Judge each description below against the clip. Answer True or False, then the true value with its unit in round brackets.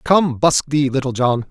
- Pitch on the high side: False (140 Hz)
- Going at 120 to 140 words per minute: False (200 wpm)